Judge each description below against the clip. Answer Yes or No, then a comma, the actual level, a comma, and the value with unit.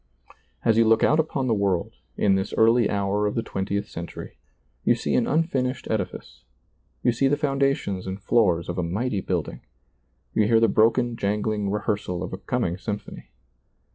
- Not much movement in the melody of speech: No, average, 3.8 semitones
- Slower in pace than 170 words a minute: No, average, 175 wpm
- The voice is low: Yes, low, 105 Hz